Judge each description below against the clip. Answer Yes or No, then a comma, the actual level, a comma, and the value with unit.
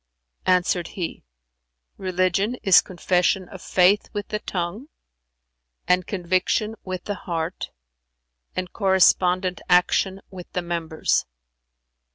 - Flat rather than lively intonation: Yes, narrow, 1.4 semitones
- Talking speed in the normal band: No, slow, 105 wpm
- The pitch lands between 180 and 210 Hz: Yes, medium, 185 Hz